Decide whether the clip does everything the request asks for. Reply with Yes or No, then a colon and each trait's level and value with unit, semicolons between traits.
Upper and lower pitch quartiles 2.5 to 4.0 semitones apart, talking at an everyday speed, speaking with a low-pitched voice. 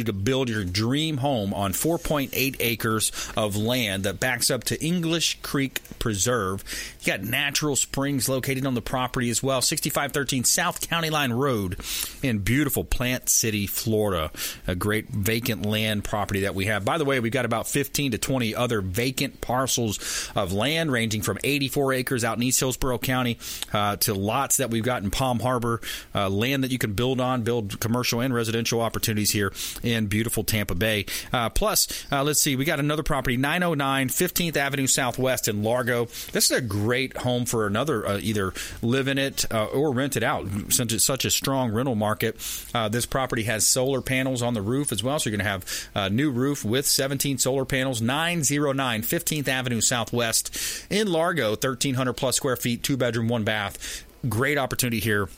Yes: average, 3.7 semitones; average, 190 wpm; low, 125 Hz